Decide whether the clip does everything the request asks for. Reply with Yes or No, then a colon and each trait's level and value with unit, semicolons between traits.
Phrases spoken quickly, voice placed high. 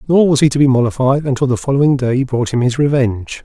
No: fast, 245 wpm; low, 130 Hz